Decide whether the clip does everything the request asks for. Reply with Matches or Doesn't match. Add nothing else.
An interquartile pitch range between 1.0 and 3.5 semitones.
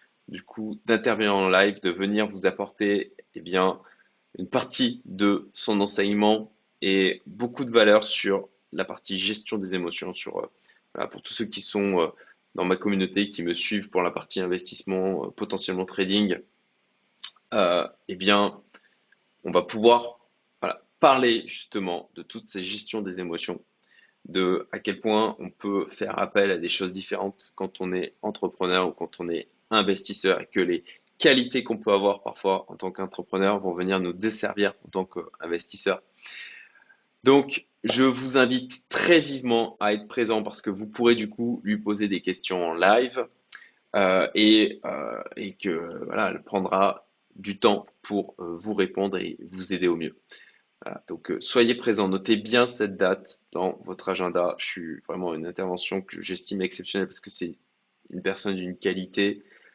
Matches